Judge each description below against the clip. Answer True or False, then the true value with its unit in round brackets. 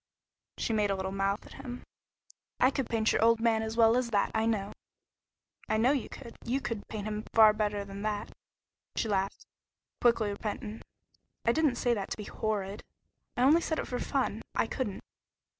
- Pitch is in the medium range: False (220 Hz)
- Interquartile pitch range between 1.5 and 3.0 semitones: True (2.5 semitones)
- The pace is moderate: True (190 wpm)